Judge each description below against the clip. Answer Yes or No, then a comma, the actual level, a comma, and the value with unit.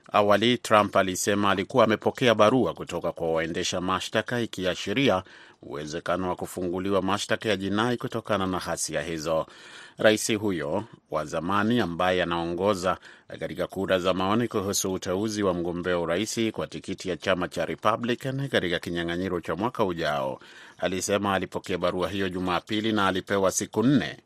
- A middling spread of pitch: Yes, average, 3.2 semitones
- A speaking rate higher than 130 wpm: Yes, fast, 140 wpm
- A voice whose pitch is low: Yes, very low, 95 Hz